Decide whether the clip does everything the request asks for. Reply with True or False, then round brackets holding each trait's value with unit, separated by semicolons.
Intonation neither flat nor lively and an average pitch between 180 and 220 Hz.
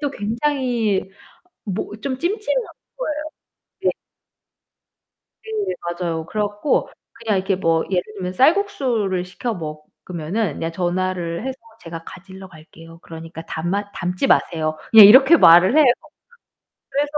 False (6.9 semitones; 190 Hz)